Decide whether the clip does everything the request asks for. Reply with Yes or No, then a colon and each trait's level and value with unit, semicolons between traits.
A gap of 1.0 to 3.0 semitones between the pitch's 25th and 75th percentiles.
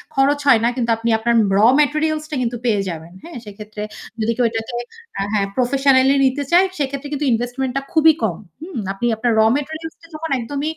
No: average, 4.4 semitones